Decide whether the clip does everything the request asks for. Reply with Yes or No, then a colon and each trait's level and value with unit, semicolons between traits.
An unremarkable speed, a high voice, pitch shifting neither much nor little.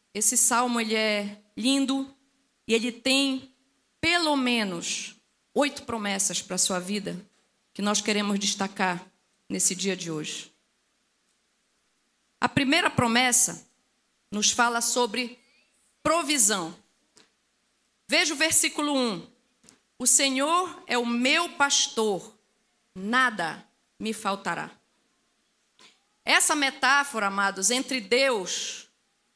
No: slow, 100 wpm; high, 235 Hz; average, 4.6 semitones